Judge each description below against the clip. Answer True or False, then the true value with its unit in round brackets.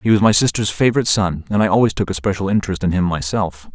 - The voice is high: False (100 Hz)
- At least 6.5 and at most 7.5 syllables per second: True (6.9 syllables/s)